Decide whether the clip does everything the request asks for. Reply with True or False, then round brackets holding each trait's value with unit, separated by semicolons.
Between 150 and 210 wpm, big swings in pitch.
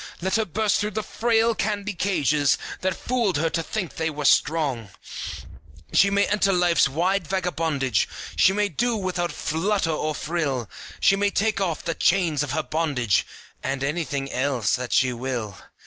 True (165 wpm; 5.8 semitones)